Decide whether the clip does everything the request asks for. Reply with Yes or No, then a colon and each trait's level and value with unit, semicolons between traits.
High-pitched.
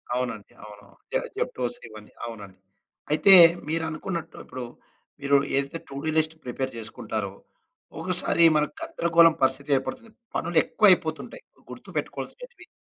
No: medium, 150 Hz